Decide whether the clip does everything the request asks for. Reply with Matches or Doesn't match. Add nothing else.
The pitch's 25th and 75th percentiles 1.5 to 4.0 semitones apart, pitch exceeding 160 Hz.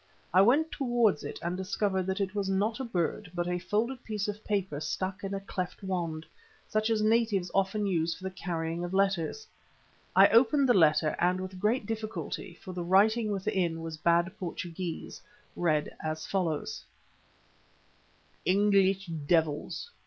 Matches